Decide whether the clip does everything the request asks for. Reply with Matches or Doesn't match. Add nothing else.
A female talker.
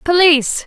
Matches